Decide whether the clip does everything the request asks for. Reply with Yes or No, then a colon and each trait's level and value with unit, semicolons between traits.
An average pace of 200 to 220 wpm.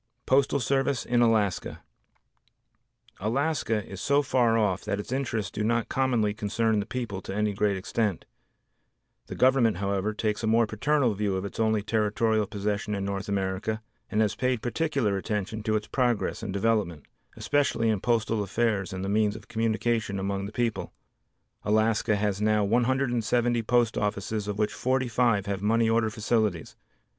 No: average, 160 wpm